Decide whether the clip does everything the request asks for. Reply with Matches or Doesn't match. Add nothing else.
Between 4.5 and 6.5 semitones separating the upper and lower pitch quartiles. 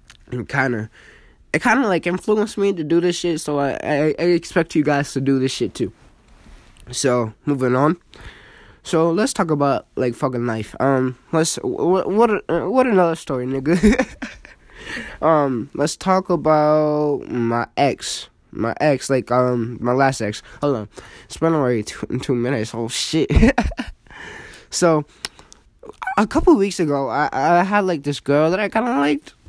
Matches